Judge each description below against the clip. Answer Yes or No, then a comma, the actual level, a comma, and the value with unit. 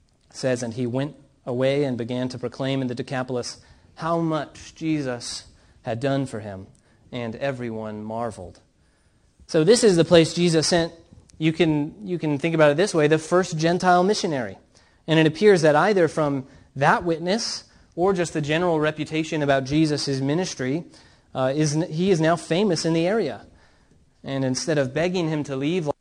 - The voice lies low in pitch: No, medium, 150 Hz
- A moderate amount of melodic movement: Yes, average, 4.3 semitones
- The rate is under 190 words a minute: Yes, average, 175 wpm